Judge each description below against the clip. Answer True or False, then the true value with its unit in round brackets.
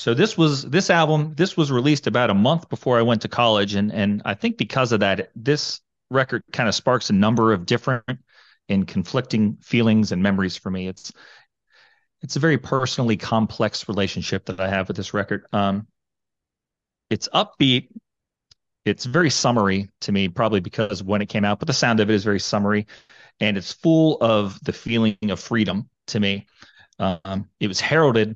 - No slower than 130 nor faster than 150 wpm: False (185 wpm)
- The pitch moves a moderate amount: True (4.7 semitones)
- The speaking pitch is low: True (110 Hz)